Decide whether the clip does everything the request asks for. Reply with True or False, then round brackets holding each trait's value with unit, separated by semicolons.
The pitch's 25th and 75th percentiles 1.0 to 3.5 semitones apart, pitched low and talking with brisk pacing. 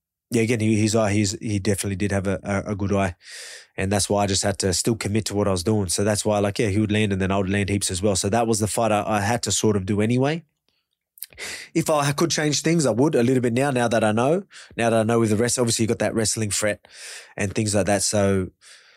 True (2.5 semitones; 105 Hz; 295 wpm)